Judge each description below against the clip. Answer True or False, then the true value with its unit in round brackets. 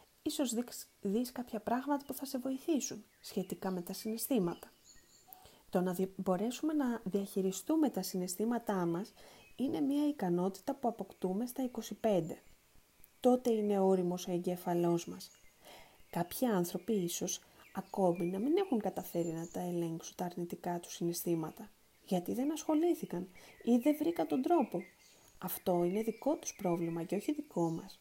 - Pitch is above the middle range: True (200 Hz)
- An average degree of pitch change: False (5.9 semitones)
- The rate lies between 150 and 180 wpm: False (140 wpm)